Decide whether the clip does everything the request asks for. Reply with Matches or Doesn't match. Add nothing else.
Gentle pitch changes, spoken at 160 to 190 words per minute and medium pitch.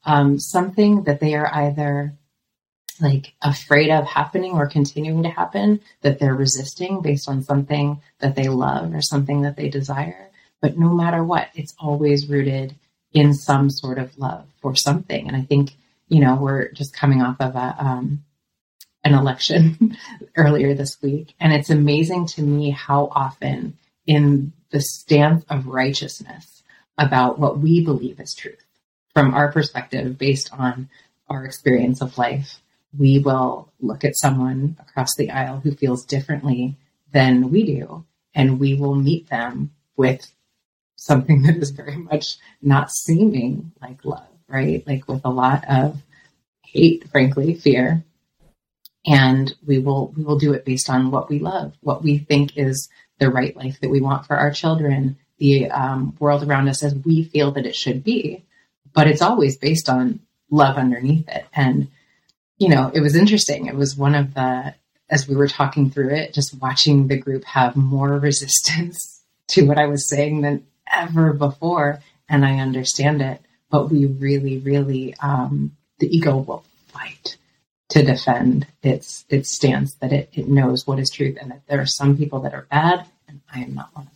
Matches